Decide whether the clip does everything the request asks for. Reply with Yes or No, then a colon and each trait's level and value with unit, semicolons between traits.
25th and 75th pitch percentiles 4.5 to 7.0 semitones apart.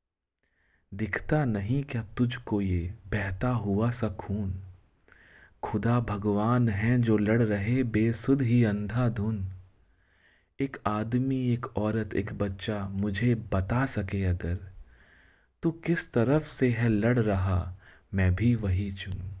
No: average, 3.9 semitones